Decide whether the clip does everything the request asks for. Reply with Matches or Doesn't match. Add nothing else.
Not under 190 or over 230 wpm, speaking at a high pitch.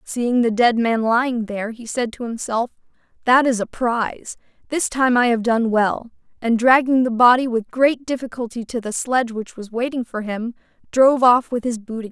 Matches